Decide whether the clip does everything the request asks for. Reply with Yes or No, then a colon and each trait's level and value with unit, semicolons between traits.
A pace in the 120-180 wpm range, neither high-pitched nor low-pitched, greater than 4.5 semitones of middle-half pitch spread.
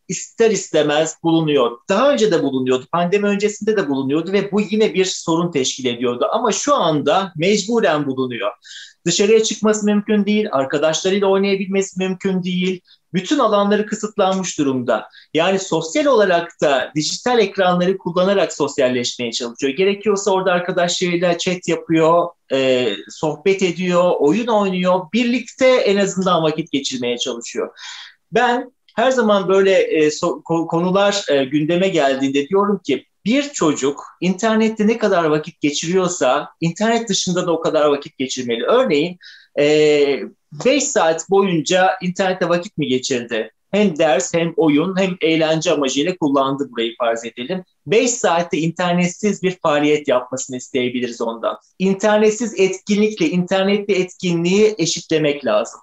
Yes: average, 125 wpm; medium, 180 Hz; average, 5.0 semitones